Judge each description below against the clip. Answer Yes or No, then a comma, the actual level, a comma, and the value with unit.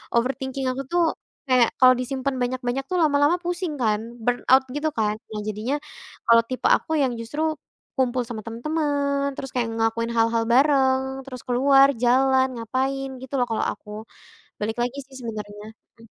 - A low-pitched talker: No, very high, 255 Hz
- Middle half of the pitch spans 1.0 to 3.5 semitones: Yes, average, 2.9 semitones